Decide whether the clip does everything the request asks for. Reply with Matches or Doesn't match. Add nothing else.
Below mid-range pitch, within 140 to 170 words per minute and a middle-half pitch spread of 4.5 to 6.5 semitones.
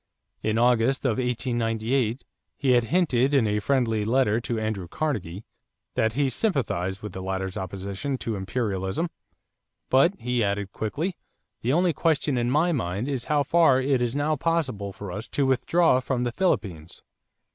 Matches